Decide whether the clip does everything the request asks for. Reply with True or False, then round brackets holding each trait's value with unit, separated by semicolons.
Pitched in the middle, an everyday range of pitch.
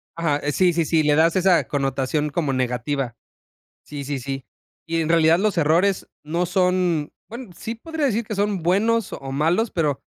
True (165 Hz; 4.5 semitones)